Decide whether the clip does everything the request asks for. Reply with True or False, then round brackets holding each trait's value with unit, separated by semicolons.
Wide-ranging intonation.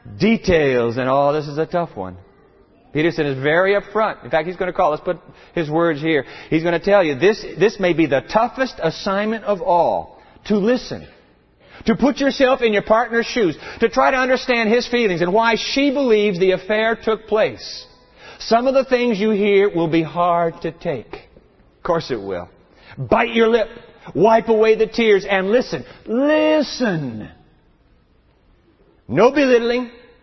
True (5.7 semitones)